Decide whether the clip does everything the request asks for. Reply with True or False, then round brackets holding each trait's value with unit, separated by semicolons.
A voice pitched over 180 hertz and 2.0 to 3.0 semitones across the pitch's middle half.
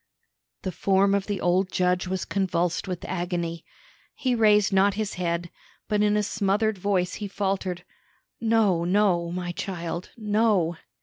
True (190 Hz; 2.7 semitones)